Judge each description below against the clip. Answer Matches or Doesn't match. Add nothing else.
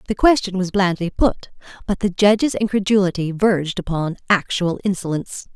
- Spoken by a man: Doesn't match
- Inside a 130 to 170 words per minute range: Matches